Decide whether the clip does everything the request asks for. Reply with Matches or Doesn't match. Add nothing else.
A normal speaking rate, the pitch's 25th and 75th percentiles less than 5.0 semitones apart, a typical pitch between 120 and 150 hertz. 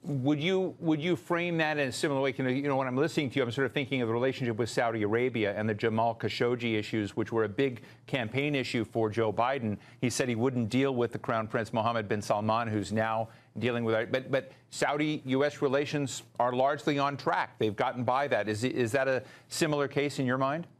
Doesn't match